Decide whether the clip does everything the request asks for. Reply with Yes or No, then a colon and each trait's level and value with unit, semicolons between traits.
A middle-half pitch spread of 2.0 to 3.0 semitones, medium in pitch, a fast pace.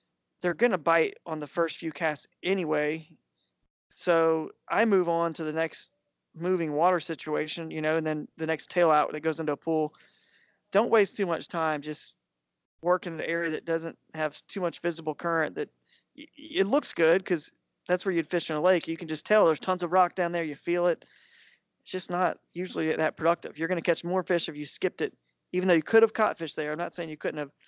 Yes: narrow, 2.5 semitones; medium, 165 Hz; fast, 230 wpm